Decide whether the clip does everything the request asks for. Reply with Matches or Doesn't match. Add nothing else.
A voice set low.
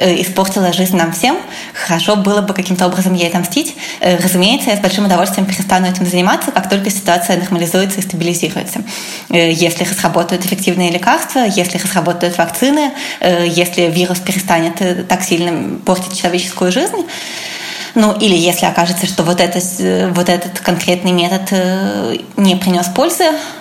Doesn't match